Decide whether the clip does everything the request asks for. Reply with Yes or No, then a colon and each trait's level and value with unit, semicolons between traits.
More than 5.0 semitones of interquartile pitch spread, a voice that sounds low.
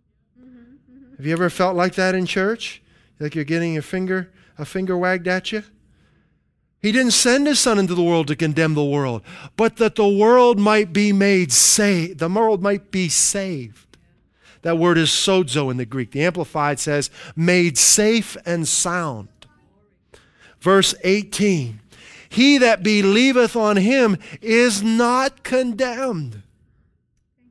No: wide, 5.5 semitones; medium, 185 Hz